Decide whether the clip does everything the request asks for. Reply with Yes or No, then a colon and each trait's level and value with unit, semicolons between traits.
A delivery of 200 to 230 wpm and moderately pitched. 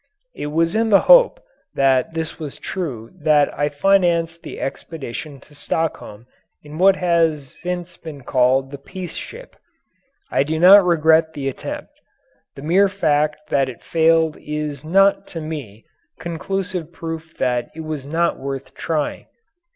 No: average, 150 wpm; medium, 160 Hz